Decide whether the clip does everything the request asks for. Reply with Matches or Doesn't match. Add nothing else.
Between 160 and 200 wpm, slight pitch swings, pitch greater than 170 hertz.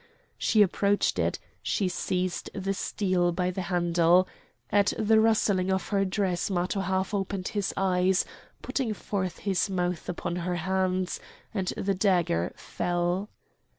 Doesn't match